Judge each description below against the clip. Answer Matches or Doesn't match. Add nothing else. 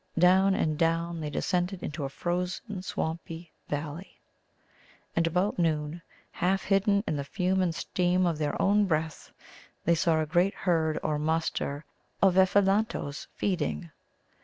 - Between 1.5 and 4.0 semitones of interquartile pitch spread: Matches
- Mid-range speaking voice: Matches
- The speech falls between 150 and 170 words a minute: Doesn't match